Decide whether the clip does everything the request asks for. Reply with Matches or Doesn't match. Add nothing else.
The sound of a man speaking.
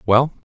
Matches